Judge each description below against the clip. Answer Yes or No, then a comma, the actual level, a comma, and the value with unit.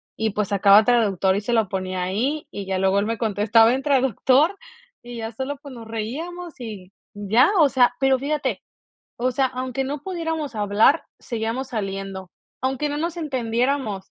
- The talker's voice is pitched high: Yes, high, 235 Hz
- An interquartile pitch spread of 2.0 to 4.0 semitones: No, average, 4.8 semitones